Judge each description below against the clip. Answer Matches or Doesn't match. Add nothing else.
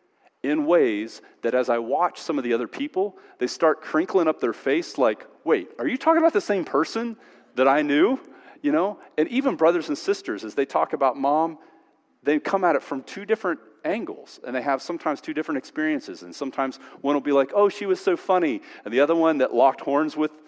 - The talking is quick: Matches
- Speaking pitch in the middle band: Matches